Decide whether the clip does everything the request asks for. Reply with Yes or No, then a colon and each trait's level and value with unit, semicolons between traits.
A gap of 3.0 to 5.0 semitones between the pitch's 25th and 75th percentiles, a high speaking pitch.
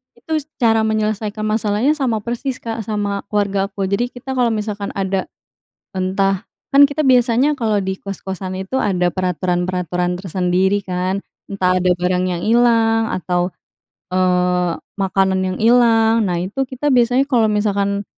Yes: average, 3.7 semitones; high, 200 Hz